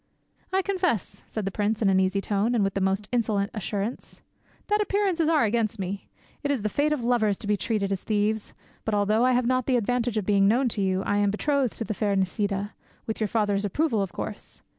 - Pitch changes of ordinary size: Yes, average, 3.7 semitones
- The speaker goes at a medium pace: No, fast, 225 wpm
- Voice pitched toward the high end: Yes, high, 215 Hz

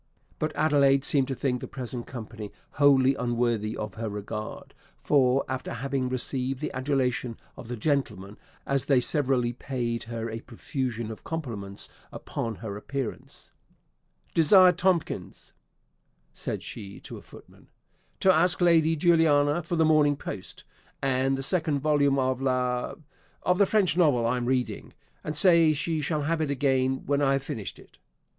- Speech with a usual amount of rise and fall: Yes, average, 3.8 semitones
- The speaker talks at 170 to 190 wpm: No, average, 160 wpm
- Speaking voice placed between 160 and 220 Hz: No, low, 135 Hz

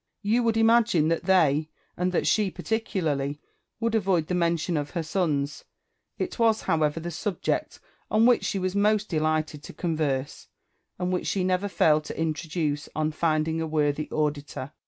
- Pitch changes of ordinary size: Yes, average, 4.2 semitones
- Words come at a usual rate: Yes, average, 165 wpm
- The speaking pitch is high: No, medium, 165 Hz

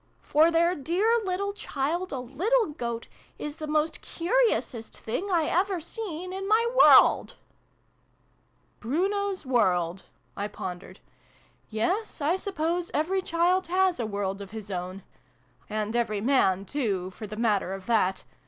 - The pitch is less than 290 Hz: No, very high, 300 Hz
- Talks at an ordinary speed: Yes, average, 145 wpm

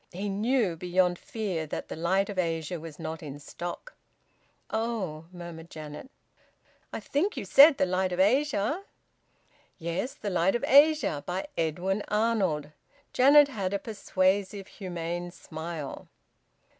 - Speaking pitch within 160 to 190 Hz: Yes, medium, 185 Hz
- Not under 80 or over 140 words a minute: Yes, slow, 135 wpm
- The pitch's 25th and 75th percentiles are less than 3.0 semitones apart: No, average, 4.8 semitones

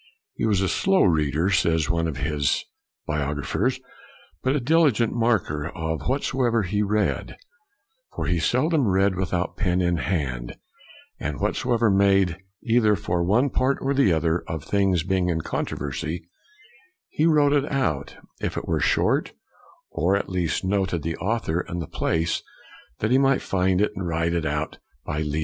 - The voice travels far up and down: Yes, wide, 6.1 semitones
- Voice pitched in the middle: No, very low, 95 Hz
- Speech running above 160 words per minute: Yes, average, 170 wpm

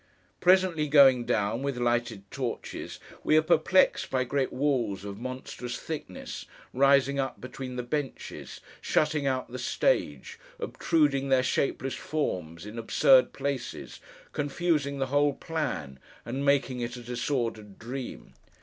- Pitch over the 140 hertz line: No, low, 135 Hz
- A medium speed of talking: No, slow, 130 wpm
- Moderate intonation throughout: Yes, average, 3.1 semitones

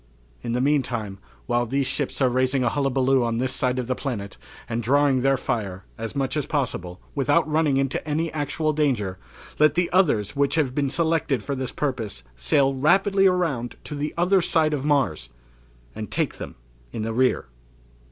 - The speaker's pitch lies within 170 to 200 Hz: No, low, 135 Hz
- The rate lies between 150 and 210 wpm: Yes, average, 180 wpm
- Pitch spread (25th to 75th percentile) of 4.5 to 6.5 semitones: No, average, 3.7 semitones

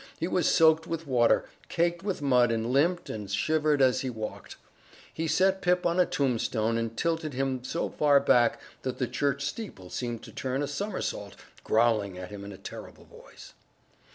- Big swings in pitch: Yes, wide, 6.0 semitones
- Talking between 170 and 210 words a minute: Yes, average, 180 wpm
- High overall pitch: No, low, 135 Hz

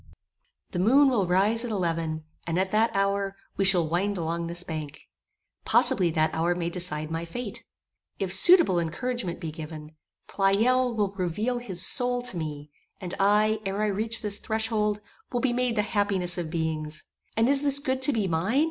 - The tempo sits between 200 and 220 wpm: No, average, 180 wpm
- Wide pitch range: No, average, 5.0 semitones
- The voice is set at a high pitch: Yes, high, 195 Hz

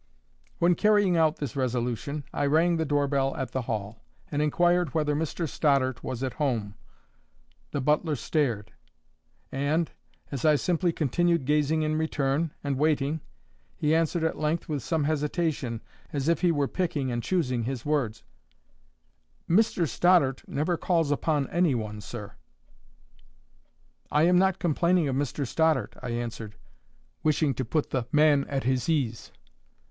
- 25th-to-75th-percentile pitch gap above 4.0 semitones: No, average, 3.7 semitones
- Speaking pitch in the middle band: Yes, medium, 145 Hz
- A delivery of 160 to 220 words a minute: No, average, 150 wpm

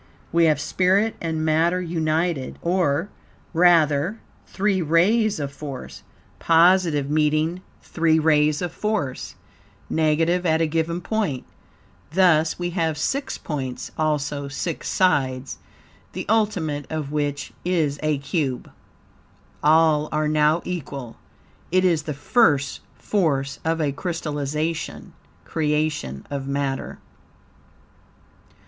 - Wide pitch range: No, average, 3.1 semitones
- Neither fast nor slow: No, slow, 110 wpm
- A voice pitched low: No, medium, 155 Hz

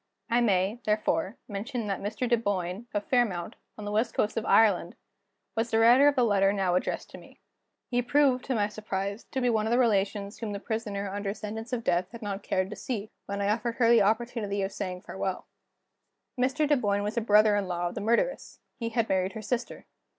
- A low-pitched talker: No, high, 215 Hz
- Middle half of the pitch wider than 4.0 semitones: No, average, 2.9 semitones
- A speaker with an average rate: No, fast, 215 wpm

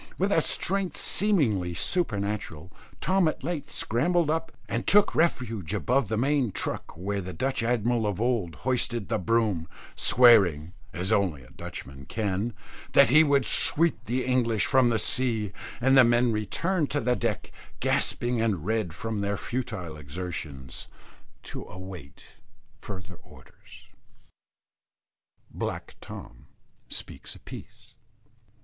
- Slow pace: Yes, slow, 130 wpm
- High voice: No, low, 115 Hz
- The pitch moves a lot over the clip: Yes, wide, 5.8 semitones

